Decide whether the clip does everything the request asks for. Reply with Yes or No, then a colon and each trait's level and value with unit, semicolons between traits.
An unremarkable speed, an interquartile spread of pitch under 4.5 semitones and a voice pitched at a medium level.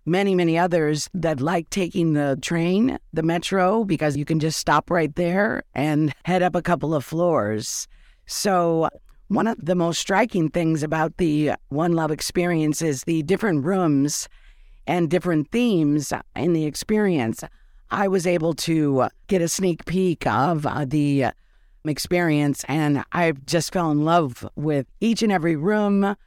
Yes: average, 155 wpm; average, 3.1 semitones; medium, 165 Hz